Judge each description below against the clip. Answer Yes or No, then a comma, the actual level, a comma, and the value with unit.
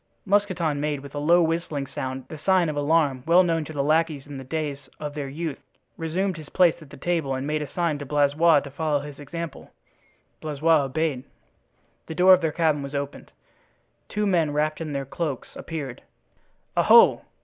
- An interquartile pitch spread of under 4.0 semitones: Yes, average, 2.7 semitones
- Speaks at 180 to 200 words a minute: Yes, average, 190 wpm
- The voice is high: No, medium, 155 Hz